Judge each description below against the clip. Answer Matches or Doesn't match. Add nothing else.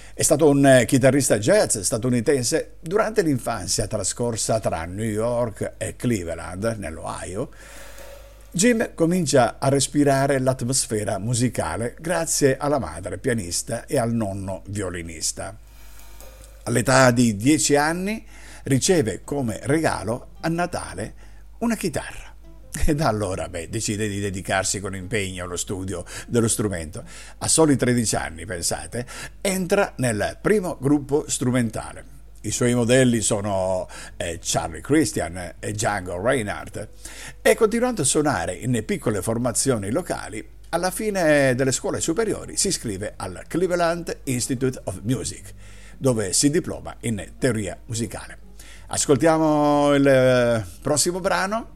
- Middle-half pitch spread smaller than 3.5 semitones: Doesn't match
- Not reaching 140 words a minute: Matches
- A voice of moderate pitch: Doesn't match